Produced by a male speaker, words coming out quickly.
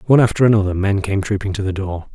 Yes: male; fast, 250 wpm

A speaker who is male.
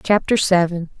No: female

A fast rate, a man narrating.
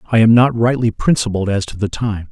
Yes: fast, 235 wpm; male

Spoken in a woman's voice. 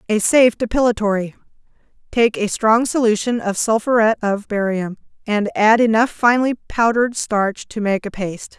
Yes: female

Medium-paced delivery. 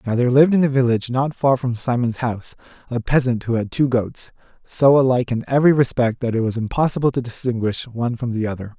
No: fast, 220 wpm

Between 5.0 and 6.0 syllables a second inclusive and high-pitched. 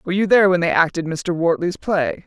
No: 5.8 syllables/s; medium, 180 Hz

